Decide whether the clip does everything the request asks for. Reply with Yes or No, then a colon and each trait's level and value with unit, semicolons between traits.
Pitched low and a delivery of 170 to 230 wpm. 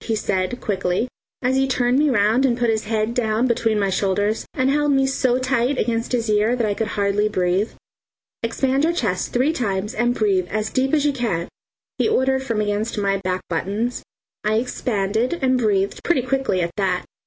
No: high, 225 Hz; average, 195 wpm